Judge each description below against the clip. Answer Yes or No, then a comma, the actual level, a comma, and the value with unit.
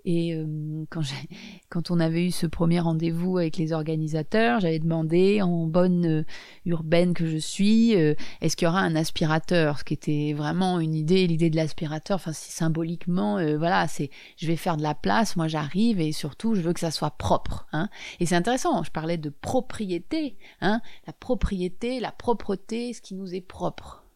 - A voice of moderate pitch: Yes, medium, 170 Hz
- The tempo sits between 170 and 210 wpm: Yes, average, 195 wpm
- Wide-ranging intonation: No, average, 3.3 semitones